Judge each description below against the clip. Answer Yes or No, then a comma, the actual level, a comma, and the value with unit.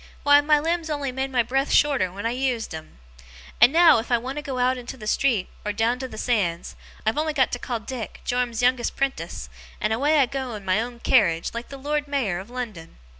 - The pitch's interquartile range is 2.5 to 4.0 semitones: Yes, average, 3.7 semitones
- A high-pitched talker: Yes, very high, 250 Hz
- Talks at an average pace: No, fast, 230 wpm